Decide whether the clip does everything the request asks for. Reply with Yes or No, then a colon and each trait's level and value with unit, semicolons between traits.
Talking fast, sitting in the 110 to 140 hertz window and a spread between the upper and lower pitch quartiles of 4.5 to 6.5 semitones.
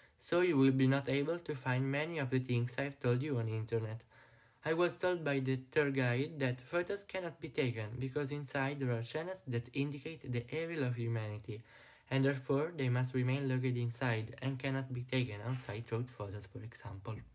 No: fast, 195 wpm; low, 130 Hz; average, 3.2 semitones